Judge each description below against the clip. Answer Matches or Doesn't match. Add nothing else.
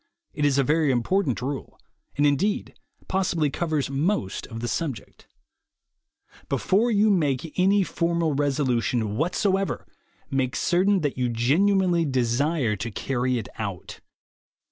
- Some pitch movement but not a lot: Doesn't match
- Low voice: Doesn't match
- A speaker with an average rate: Doesn't match